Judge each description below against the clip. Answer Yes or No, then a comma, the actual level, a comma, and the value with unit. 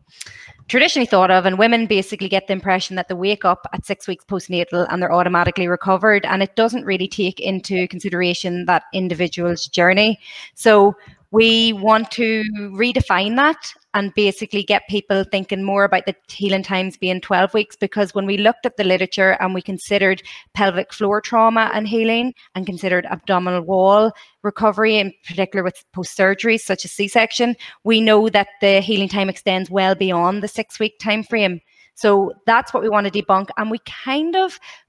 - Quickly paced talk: No, average, 175 wpm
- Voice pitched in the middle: No, high, 200 Hz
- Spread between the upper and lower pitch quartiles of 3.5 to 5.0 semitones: No, narrow, 2.5 semitones